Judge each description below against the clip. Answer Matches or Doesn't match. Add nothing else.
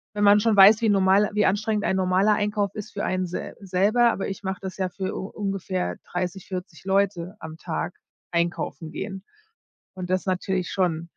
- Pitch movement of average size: Doesn't match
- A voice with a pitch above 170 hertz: Matches